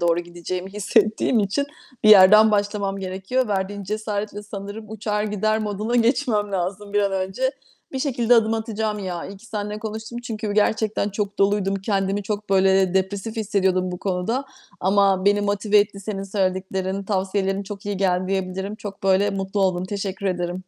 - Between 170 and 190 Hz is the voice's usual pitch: No, high, 200 Hz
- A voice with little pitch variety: Yes, narrow, 1.8 semitones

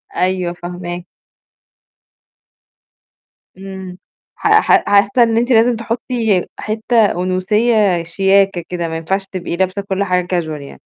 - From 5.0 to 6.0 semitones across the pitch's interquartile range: No, average, 3.5 semitones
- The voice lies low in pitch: No, high, 190 Hz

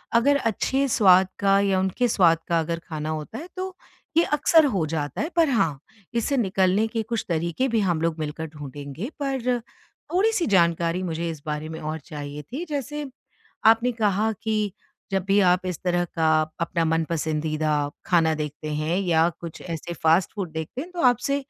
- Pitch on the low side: No, medium, 180 Hz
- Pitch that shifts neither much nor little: No, wide, 6.5 semitones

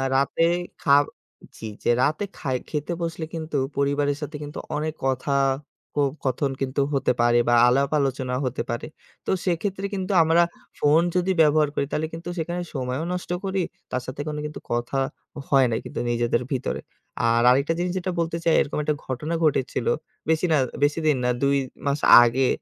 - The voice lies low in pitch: No, medium, 145 Hz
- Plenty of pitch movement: No, average, 3.8 semitones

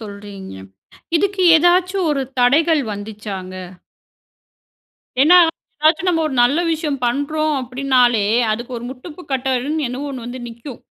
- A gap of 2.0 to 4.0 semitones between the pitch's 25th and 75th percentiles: No, average, 4.6 semitones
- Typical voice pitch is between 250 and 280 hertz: Yes, very high, 270 Hz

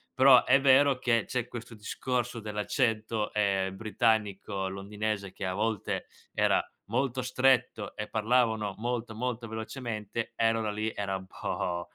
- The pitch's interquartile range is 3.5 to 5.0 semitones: No, average, 2.9 semitones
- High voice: No, low, 110 Hz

